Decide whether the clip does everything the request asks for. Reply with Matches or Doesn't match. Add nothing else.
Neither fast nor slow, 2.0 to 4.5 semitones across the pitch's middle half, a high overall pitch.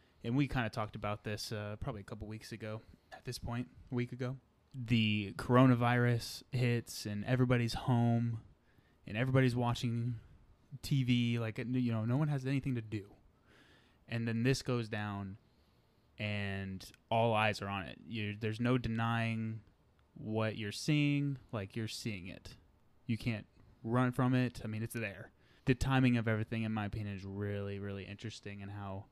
Doesn't match